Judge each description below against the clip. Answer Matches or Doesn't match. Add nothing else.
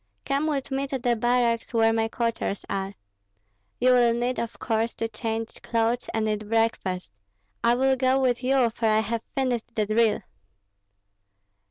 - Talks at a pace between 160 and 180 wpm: Matches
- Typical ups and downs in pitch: Doesn't match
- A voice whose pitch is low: Doesn't match